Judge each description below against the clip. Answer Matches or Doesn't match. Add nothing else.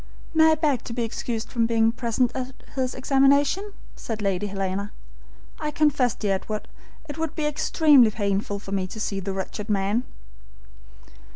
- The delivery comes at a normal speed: Matches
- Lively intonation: Matches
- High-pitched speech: Matches